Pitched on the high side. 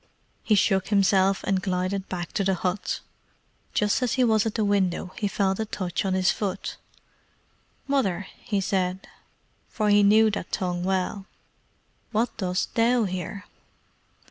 Yes: high, 195 Hz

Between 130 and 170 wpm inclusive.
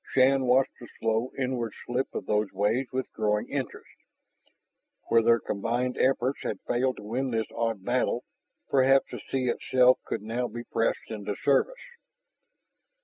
Yes: average, 150 wpm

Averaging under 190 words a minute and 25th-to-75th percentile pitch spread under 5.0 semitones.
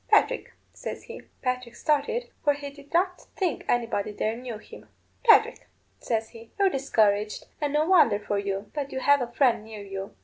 No: average, 180 wpm; wide, 5.4 semitones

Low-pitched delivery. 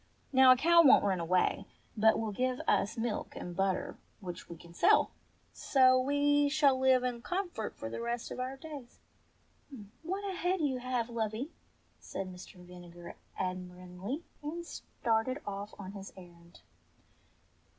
No: high, 235 Hz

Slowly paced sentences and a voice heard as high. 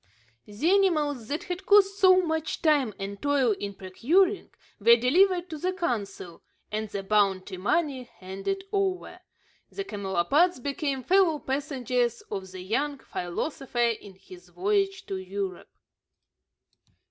Yes: slow, 130 wpm; very high, 265 Hz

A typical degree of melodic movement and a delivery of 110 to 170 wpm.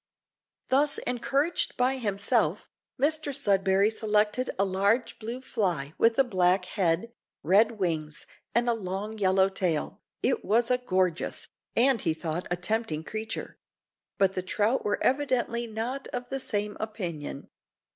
Yes: average, 4.7 semitones; average, 140 wpm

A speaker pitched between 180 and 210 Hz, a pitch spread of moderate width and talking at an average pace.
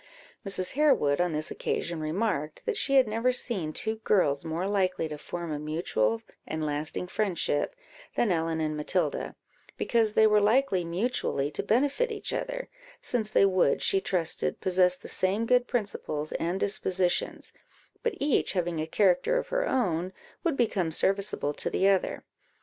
No: high, 190 Hz; wide, 6.1 semitones; average, 160 wpm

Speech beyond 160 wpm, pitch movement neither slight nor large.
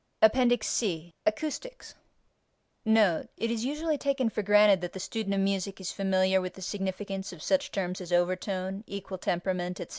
Yes: average, 175 wpm; average, 3.2 semitones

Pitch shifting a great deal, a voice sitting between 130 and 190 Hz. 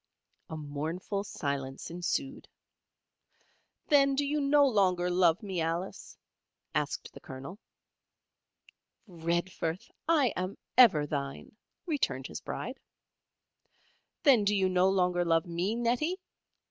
Yes: wide, 6.4 semitones; medium, 185 Hz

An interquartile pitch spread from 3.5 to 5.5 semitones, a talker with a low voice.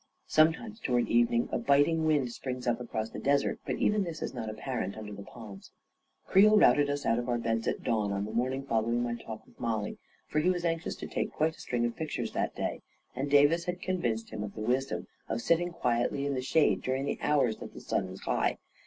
Yes: average, 5.2 semitones; low, 130 Hz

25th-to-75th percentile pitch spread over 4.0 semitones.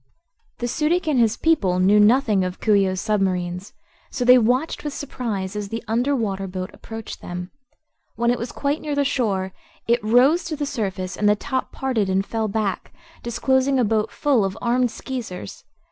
Yes: average, 5.1 semitones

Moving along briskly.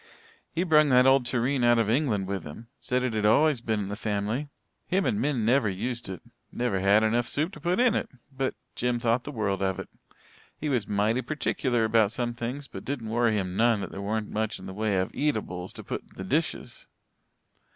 Yes: fast, 215 wpm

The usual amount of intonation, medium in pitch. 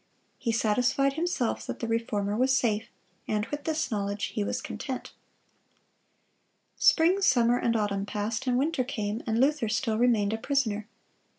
No: average, 3.9 semitones; high, 230 Hz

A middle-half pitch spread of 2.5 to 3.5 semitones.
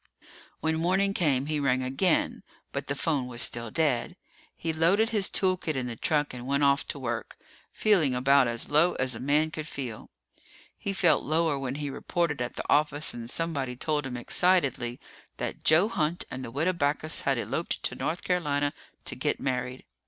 No: average, 4.2 semitones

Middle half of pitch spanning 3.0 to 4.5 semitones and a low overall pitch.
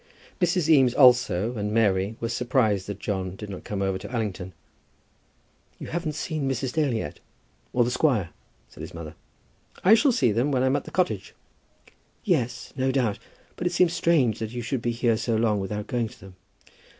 No: average, 4.9 semitones; low, 120 Hz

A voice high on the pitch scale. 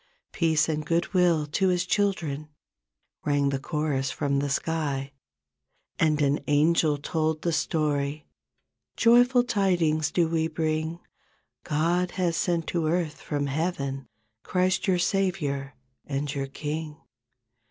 No: medium, 155 Hz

